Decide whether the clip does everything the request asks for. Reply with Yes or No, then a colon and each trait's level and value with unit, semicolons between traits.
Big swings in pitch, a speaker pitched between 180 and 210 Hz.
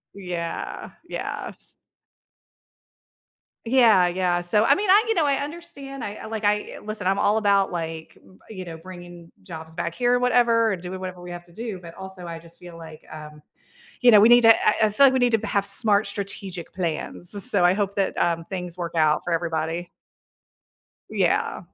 No: average, 4.3 semitones; high, 190 Hz